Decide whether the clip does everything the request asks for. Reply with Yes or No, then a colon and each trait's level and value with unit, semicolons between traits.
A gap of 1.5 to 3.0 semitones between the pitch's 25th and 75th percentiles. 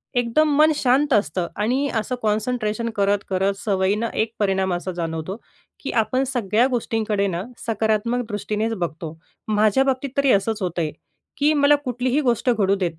No: average, 4.4 semitones